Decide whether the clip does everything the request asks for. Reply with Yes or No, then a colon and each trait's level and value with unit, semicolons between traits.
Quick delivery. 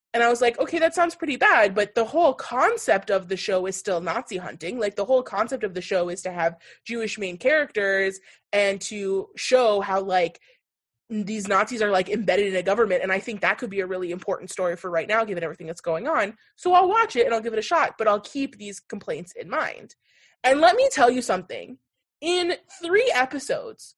Yes: fast, 225 wpm